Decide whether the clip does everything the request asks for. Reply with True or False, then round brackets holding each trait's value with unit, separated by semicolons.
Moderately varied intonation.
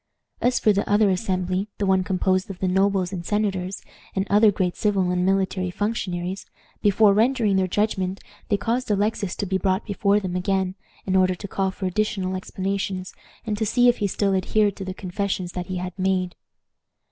False (1.8 semitones)